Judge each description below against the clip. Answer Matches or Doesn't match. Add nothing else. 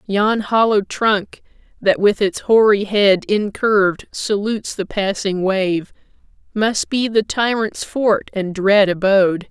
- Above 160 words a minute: Doesn't match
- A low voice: Doesn't match